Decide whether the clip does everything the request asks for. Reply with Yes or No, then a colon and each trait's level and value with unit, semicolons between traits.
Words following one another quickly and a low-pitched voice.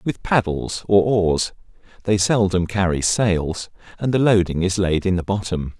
No: average, 165 wpm; very low, 95 Hz